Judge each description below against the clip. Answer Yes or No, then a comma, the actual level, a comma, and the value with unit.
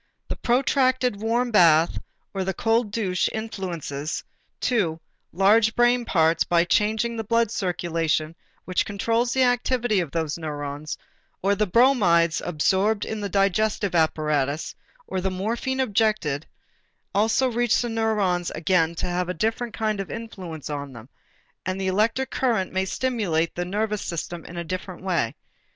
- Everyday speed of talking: Yes, average, 150 wpm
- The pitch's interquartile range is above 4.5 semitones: Yes, average, 5.0 semitones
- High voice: Yes, high, 195 Hz